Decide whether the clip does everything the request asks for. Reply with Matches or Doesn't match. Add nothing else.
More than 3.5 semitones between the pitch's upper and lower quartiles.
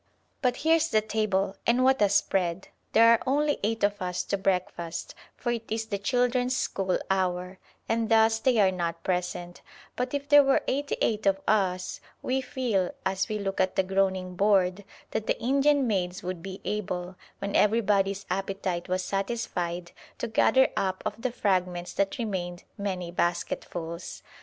Matches